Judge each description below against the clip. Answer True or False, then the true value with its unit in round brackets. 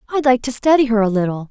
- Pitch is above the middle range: True (240 Hz)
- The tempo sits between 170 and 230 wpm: False (280 wpm)